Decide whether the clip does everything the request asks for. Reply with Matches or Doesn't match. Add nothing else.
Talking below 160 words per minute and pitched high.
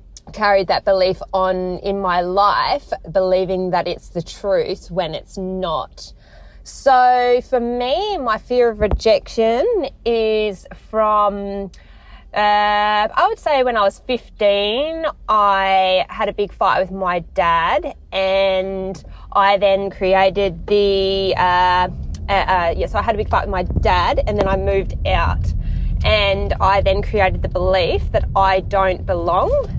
Matches